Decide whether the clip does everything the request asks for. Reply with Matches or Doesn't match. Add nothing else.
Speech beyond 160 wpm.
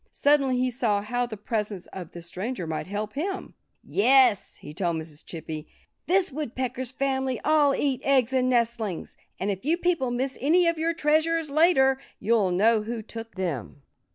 Matches